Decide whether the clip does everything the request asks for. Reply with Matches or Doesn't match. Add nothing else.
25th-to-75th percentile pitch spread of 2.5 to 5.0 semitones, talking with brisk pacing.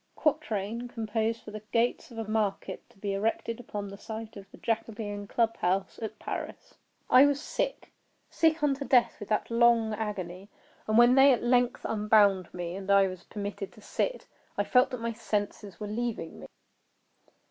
Doesn't match